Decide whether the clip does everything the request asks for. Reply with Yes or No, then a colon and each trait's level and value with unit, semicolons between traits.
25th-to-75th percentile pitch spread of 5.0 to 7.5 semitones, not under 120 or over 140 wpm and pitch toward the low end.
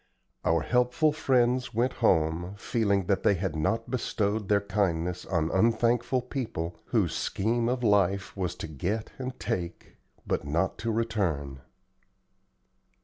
Yes: wide, 5.4 semitones; slow, 135 wpm; low, 100 Hz